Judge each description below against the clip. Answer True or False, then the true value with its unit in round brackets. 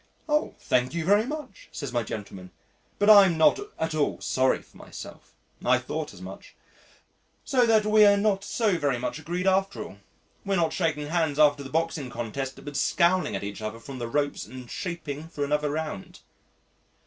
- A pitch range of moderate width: False (6.2 semitones)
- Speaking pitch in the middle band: True (155 Hz)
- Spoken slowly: False (185 wpm)